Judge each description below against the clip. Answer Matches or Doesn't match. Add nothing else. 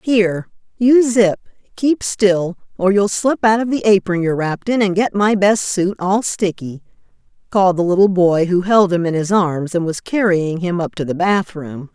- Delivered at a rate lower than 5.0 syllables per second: Matches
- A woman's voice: Matches